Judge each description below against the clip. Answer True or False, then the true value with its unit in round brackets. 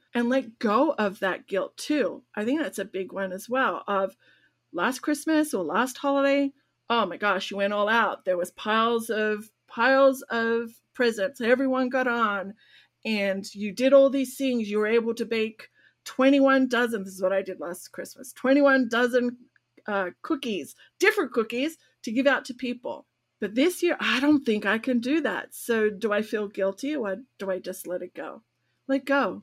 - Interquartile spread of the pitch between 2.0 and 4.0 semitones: False (4.7 semitones)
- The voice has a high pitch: True (235 Hz)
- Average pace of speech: True (190 wpm)